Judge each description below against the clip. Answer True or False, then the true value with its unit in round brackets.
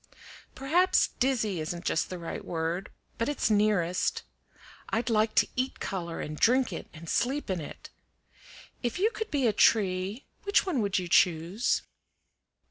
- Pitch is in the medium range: False (210 Hz)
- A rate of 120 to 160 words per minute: True (155 wpm)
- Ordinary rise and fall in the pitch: False (6.6 semitones)